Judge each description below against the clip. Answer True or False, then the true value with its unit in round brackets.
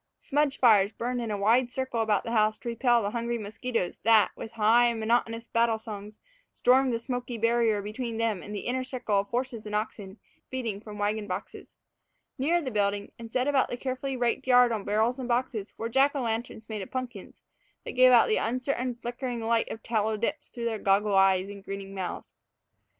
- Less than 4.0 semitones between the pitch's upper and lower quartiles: True (2.9 semitones)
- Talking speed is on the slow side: False (200 wpm)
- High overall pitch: True (230 Hz)